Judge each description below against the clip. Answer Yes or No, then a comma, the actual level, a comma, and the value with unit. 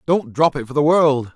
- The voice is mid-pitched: Yes, medium, 145 Hz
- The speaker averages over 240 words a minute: Yes, fast, 265 wpm